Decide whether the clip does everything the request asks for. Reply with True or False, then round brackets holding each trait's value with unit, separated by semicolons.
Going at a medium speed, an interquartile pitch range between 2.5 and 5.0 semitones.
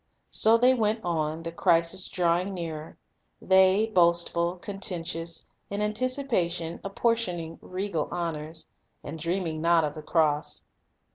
False (120 wpm; 3.1 semitones)